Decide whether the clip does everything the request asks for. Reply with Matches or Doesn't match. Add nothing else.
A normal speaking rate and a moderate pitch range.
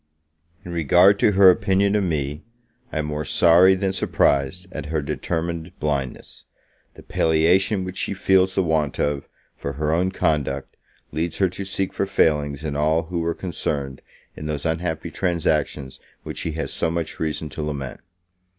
Matches